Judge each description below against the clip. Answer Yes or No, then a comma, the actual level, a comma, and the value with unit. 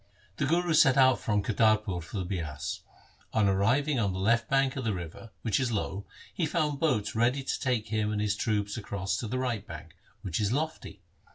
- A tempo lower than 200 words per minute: No, fast, 205 wpm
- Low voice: Yes, low, 110 Hz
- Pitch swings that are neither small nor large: Yes, average, 4.7 semitones